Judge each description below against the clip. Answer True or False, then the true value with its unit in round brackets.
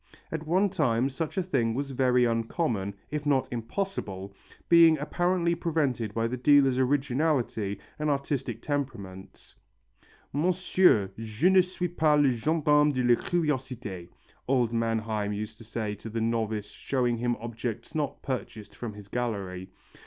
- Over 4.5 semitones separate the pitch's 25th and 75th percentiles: True (5.1 semitones)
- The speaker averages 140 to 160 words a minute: True (145 wpm)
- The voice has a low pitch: True (125 Hz)